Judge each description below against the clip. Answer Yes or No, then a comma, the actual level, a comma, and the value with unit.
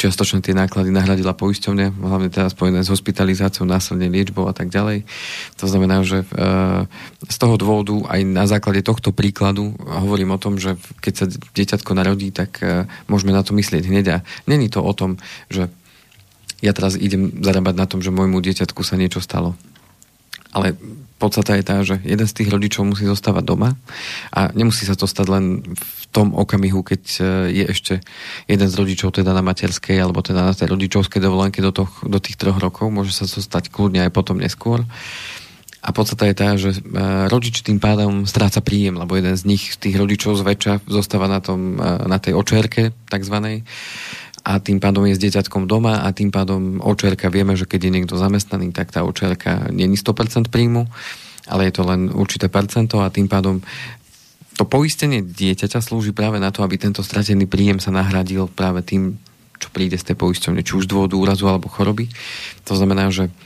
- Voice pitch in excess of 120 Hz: No, very low, 95 Hz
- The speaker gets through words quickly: Yes, fast, 185 wpm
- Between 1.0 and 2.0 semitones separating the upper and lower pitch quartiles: Yes, narrow, 1.5 semitones